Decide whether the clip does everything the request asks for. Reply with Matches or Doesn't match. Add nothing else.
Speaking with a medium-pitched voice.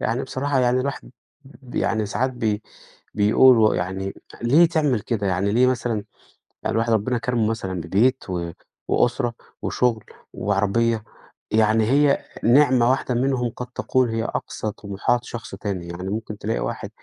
Doesn't match